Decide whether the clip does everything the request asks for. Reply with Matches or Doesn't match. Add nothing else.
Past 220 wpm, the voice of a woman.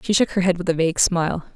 Matches